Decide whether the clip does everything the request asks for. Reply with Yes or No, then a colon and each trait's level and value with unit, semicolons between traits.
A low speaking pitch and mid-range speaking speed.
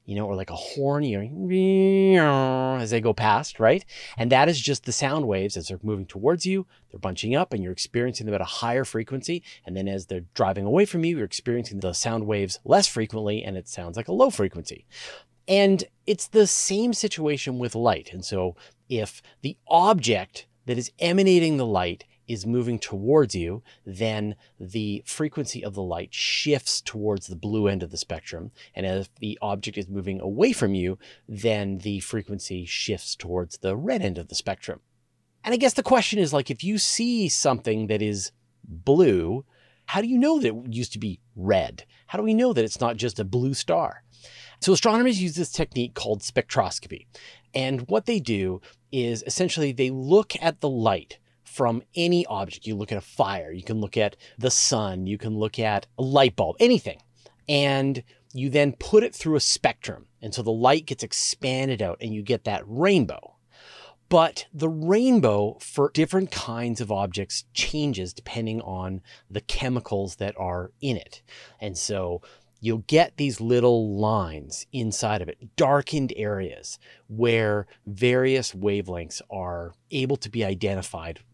Yes: low, 115 Hz; average, 180 wpm